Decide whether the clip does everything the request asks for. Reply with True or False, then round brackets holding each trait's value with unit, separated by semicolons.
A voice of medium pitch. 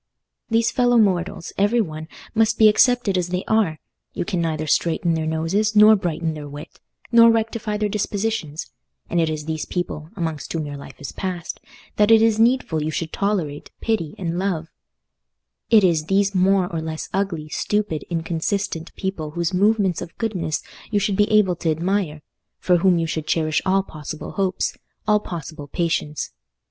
True (180 Hz)